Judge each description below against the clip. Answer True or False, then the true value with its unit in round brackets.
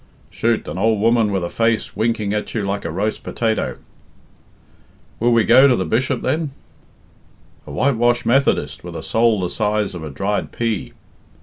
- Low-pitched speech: True (110 Hz)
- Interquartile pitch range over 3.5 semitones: False (2.8 semitones)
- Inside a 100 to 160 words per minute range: False (175 wpm)